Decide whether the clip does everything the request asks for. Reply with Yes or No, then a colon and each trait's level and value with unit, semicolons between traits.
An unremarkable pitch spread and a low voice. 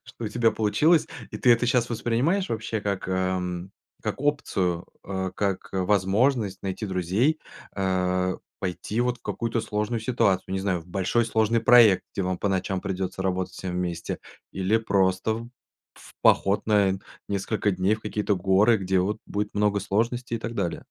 Yes: average, 3.4 semitones; low, 100 Hz